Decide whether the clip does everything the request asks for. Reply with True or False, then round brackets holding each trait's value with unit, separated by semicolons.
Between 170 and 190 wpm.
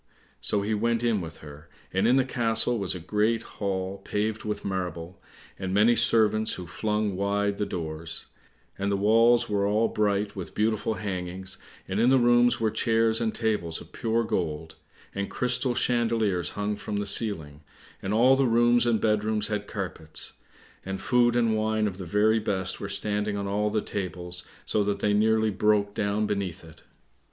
True (180 wpm)